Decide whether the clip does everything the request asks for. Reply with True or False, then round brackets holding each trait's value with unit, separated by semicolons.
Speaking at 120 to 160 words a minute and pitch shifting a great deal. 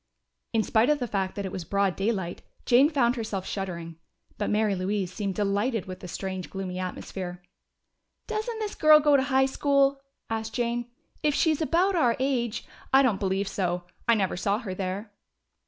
False (185 wpm; 5.8 semitones)